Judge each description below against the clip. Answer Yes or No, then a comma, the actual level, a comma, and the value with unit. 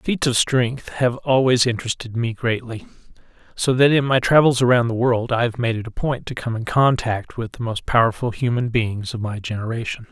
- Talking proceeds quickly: Yes, fast, 210 wpm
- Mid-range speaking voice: No, low, 120 Hz